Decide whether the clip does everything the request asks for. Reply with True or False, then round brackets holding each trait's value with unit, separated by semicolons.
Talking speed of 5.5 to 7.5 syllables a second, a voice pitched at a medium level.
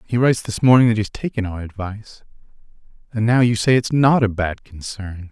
False (5.6 syllables/s; 110 Hz)